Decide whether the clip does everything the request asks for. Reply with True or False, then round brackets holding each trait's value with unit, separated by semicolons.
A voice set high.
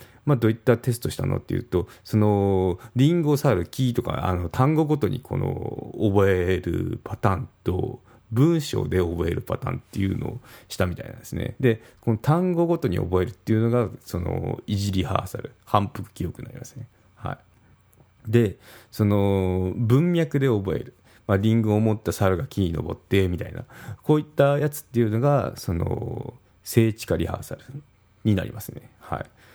False (115 Hz)